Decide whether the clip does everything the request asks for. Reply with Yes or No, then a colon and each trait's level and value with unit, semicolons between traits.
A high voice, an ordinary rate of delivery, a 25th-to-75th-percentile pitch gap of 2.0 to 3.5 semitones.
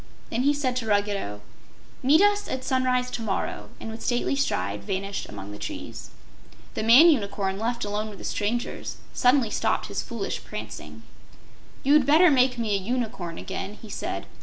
No: high, 230 Hz; average, 170 wpm; average, 4.3 semitones